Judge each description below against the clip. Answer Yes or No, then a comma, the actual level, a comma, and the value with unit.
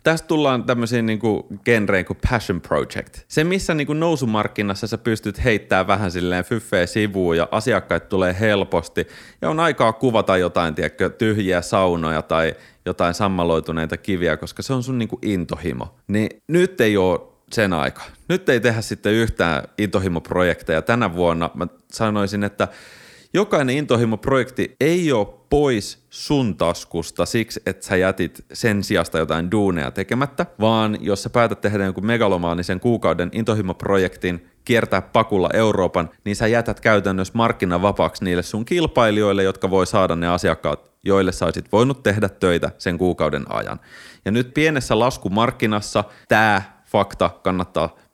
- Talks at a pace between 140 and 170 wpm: Yes, average, 145 wpm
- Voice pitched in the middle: No, low, 105 Hz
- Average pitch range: Yes, average, 4.4 semitones